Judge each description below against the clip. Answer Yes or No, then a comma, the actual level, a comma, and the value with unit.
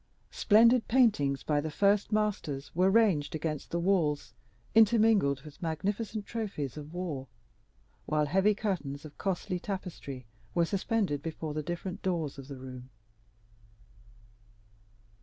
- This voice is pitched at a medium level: Yes, medium, 170 Hz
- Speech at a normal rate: No, slow, 125 wpm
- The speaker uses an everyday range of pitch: No, wide, 5.9 semitones